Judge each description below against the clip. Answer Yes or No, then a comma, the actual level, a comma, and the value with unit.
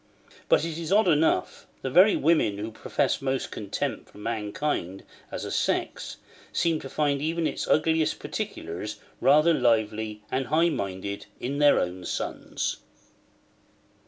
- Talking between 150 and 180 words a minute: No, average, 140 wpm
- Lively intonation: Yes, wide, 7.1 semitones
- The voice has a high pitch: No, low, 135 Hz